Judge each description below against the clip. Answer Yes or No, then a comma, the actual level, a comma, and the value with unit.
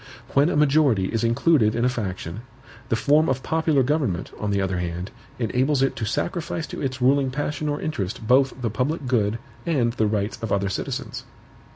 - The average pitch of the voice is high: No, low, 125 Hz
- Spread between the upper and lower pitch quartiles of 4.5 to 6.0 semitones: Yes, wide, 5.5 semitones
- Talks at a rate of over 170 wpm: Yes, average, 190 wpm